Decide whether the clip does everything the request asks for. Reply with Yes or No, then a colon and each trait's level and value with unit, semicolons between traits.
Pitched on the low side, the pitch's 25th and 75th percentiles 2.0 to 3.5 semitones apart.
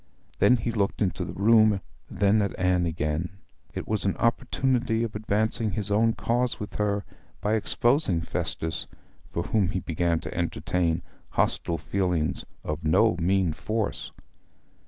No: low, 100 Hz; average, 4.3 semitones